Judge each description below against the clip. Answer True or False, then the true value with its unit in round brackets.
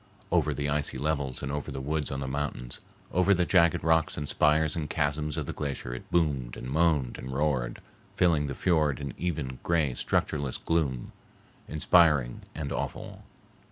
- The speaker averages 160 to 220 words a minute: True (170 wpm)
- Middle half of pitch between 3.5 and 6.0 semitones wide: False (2.9 semitones)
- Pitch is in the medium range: False (75 Hz)